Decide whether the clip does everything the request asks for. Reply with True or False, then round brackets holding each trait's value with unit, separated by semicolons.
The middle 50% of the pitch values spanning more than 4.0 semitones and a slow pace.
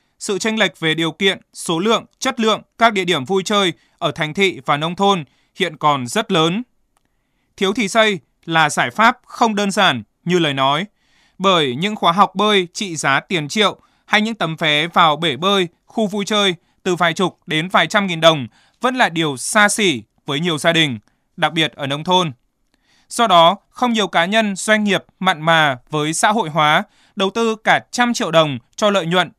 False (4.8 semitones; 205 wpm)